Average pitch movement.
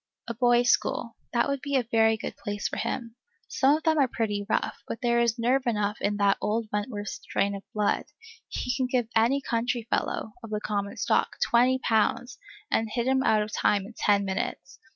Yes: average, 3.0 semitones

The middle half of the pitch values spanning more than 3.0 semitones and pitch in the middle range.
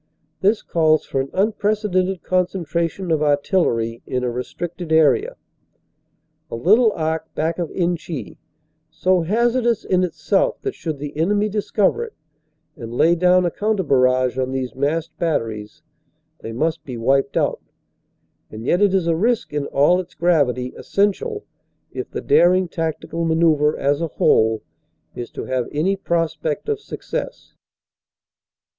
Yes: average, 5.2 semitones; medium, 165 Hz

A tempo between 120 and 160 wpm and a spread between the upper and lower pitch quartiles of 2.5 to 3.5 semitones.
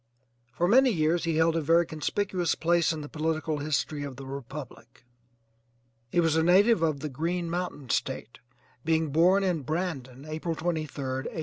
No: average, 170 wpm; average, 3.0 semitones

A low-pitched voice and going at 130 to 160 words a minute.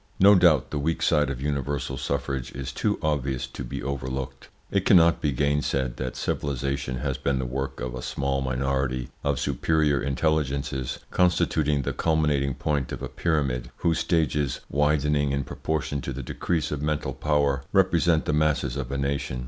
No: very low, 70 Hz; average, 170 wpm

